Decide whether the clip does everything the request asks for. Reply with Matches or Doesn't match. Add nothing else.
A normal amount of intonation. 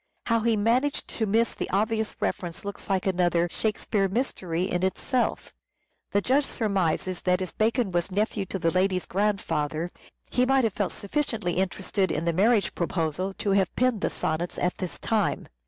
Matches